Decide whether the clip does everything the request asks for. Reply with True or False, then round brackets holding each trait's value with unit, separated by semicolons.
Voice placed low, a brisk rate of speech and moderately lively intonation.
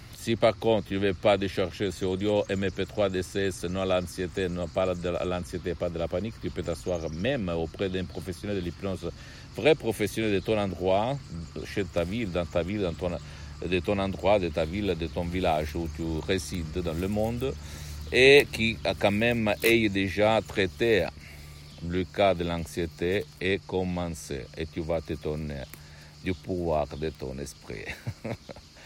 True (90 Hz; 175 wpm; 3.3 semitones)